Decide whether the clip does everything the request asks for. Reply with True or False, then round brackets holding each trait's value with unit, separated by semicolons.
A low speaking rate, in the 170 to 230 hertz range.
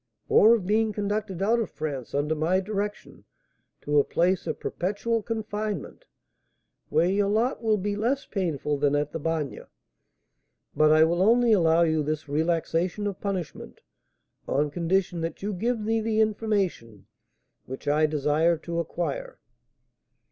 False (150 wpm; 185 Hz)